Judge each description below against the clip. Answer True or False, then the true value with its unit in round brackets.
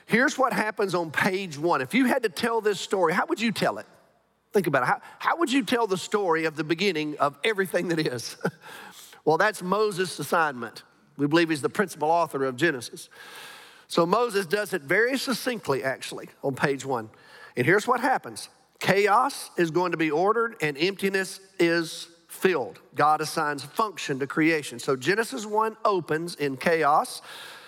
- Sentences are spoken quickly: False (180 wpm)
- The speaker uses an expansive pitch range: True (5.8 semitones)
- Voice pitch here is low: False (180 Hz)